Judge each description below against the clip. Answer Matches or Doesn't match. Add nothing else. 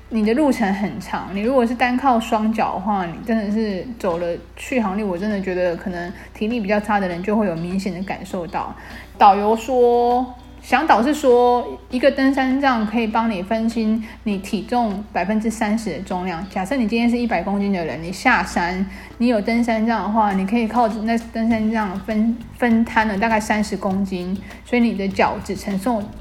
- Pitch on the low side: Doesn't match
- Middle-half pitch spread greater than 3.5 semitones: Doesn't match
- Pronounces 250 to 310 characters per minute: Matches